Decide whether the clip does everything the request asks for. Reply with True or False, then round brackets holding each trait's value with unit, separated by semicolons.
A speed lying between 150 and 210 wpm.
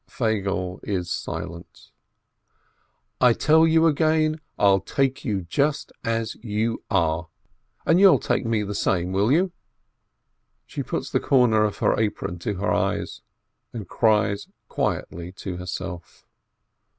False (140 wpm)